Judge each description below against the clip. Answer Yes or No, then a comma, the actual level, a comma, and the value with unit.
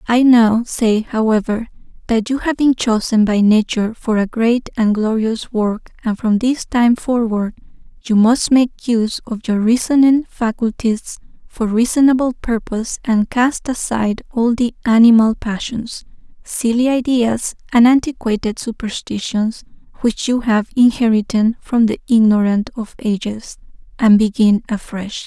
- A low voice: No, high, 230 Hz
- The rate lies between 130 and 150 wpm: Yes, slow, 135 wpm